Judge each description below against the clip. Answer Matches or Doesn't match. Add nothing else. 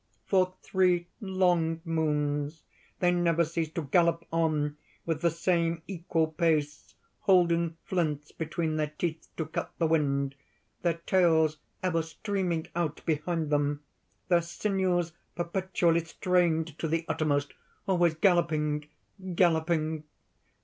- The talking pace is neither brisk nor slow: Doesn't match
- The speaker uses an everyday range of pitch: Doesn't match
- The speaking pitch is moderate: Matches